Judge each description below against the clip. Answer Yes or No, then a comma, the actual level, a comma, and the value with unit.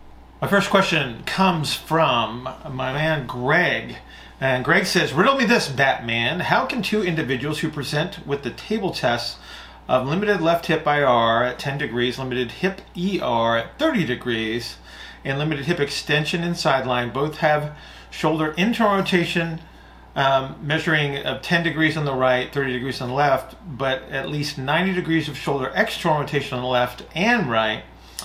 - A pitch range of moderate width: Yes, average, 4.6 semitones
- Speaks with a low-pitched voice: No, medium, 150 Hz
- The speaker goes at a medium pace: Yes, average, 165 wpm